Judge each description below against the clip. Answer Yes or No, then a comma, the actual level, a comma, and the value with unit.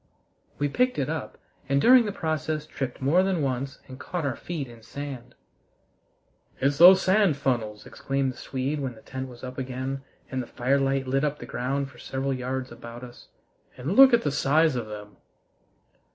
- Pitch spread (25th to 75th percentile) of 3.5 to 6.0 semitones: No, average, 3.0 semitones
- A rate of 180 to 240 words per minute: Yes, average, 185 wpm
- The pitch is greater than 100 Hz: Yes, low, 135 Hz